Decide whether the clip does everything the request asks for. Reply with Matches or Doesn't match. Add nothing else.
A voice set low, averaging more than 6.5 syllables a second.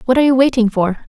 Doesn't match